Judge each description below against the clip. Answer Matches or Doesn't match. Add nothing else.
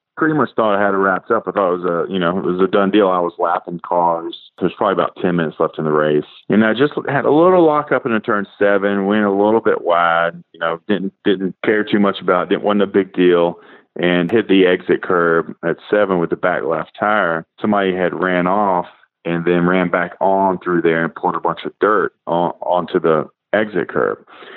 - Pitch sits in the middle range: Doesn't match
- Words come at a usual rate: Doesn't match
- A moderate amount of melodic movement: Matches